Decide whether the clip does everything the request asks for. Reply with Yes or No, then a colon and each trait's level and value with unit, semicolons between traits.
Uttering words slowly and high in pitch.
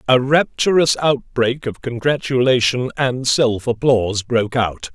No: slow, 120 wpm; low, 125 Hz